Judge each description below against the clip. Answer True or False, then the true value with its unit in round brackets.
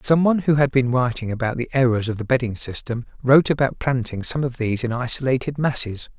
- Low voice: True (125 Hz)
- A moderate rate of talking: False (215 wpm)